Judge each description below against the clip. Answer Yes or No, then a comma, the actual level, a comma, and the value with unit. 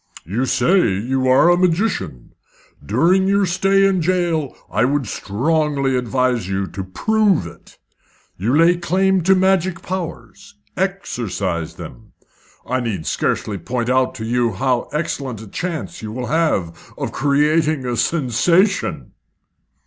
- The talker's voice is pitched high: No, medium, 140 Hz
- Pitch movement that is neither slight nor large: No, wide, 7.3 semitones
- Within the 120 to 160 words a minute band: Yes, slow, 135 wpm